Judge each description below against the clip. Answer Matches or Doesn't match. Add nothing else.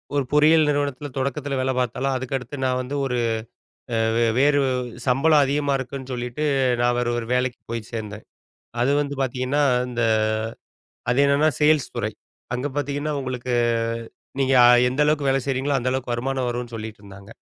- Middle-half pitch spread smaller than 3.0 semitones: Matches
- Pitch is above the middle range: Doesn't match